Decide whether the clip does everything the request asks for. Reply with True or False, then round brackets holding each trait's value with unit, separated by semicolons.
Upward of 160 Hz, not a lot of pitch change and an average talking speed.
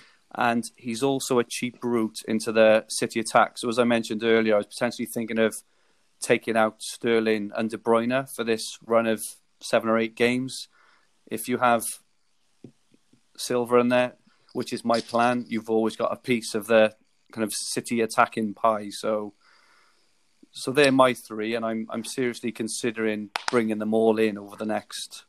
False (115 Hz; 1.6 semitones; 175 wpm)